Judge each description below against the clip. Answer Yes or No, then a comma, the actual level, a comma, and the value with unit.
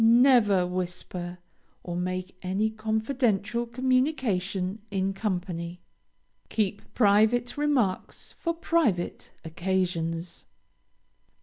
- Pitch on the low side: No, high, 200 Hz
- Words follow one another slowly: Yes, slow, 80 wpm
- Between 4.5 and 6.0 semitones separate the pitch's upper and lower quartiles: Yes, average, 4.8 semitones